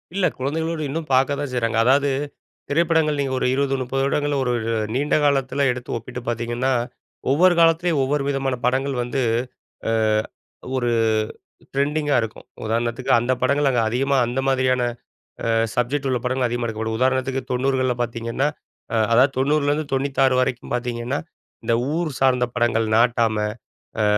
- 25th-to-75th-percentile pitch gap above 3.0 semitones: No, narrow, 2.6 semitones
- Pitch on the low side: Yes, low, 130 Hz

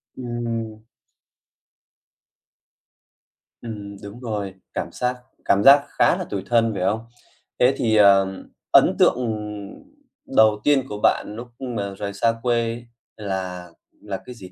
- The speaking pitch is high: No, low, 110 Hz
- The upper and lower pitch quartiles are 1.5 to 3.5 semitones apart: Yes, average, 3.0 semitones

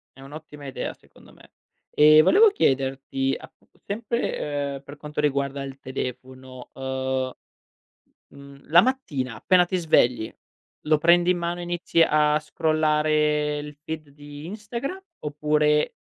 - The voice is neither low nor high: Yes, medium, 150 Hz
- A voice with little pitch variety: No, average, 3.1 semitones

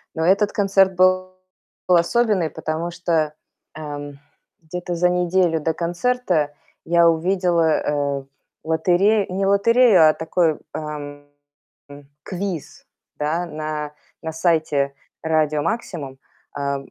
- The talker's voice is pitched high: No, medium, 170 Hz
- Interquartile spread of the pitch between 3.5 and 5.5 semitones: No, average, 3.1 semitones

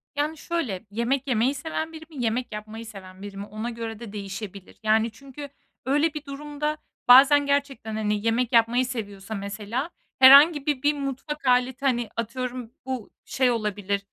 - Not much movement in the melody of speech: No, average, 4.5 semitones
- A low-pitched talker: No, high, 245 Hz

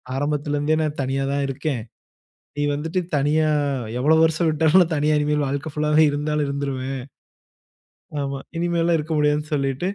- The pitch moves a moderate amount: No, narrow, 1.9 semitones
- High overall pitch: No, medium, 150 Hz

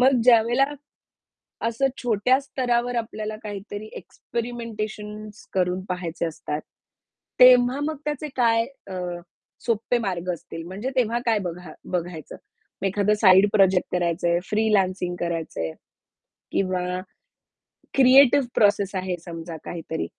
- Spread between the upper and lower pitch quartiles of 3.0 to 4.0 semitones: No, average, 4.8 semitones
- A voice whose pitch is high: Yes, high, 210 Hz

